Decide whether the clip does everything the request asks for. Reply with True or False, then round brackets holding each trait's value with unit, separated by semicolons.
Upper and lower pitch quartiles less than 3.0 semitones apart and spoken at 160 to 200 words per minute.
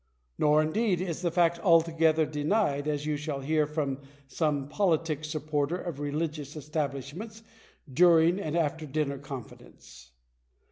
False (2.4 semitones; 135 wpm)